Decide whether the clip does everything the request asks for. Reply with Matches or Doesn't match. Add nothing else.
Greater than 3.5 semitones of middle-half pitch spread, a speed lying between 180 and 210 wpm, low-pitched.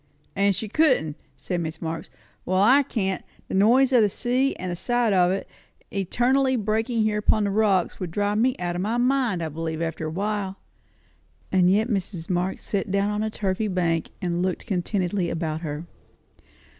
Doesn't match